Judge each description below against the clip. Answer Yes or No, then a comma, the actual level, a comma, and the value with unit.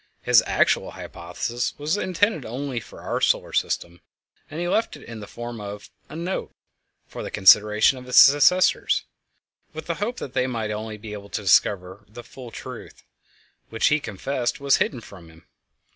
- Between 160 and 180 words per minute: Yes, average, 175 wpm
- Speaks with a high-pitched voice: No, low, 120 Hz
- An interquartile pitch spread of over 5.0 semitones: Yes, wide, 5.5 semitones